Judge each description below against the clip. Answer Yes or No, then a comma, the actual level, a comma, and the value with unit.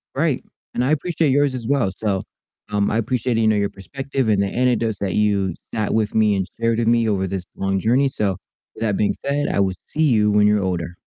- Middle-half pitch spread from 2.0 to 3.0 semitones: No, average, 4.0 semitones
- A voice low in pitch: Yes, low, 110 Hz